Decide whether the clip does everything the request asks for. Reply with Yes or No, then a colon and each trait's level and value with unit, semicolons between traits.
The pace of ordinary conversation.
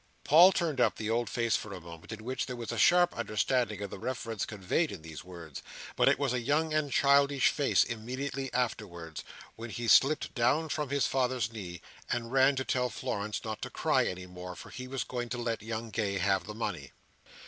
No: fast, 215 wpm